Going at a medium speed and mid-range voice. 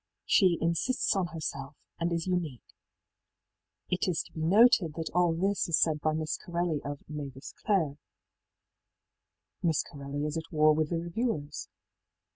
Yes: average, 150 wpm; medium, 165 Hz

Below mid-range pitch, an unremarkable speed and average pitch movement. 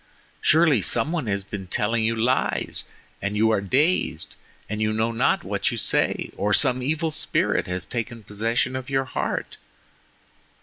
Yes: low, 115 Hz; average, 160 wpm; average, 4.1 semitones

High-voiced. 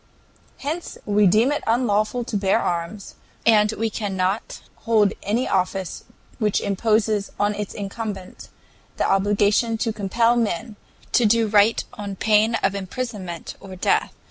Yes: high, 210 Hz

